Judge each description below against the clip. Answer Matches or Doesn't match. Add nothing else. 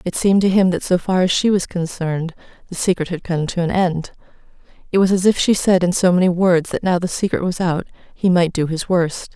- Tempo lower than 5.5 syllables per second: Doesn't match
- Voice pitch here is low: Doesn't match